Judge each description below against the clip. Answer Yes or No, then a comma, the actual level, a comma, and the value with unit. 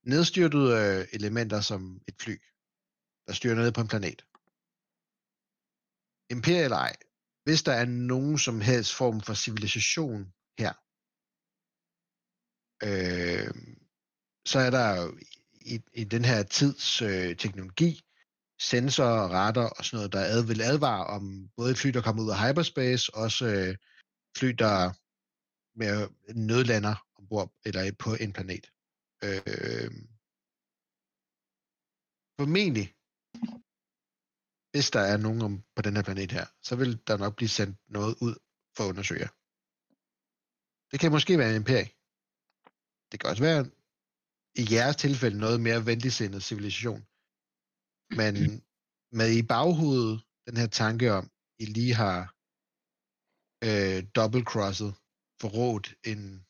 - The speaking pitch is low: Yes, low, 115 Hz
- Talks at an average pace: No, slow, 125 wpm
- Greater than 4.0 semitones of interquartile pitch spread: No, average, 3.7 semitones